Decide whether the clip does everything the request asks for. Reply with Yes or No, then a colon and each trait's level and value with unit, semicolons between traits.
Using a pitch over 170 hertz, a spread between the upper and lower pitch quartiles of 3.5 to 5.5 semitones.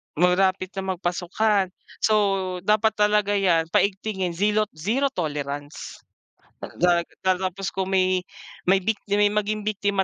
No: high, 190 Hz; narrow, 2.6 semitones